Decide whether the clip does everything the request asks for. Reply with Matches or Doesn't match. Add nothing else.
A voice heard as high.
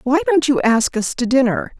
Matches